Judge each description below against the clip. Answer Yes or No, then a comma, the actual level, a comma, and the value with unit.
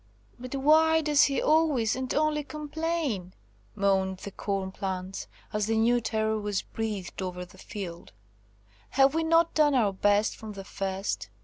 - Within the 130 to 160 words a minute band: Yes, average, 155 wpm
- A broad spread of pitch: Yes, wide, 7.2 semitones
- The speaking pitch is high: Yes, high, 220 Hz